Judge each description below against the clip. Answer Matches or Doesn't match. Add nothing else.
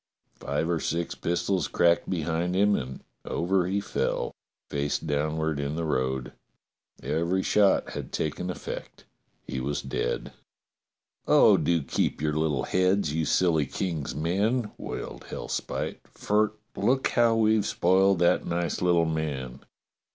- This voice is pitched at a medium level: Doesn't match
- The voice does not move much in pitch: Doesn't match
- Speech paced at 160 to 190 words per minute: Doesn't match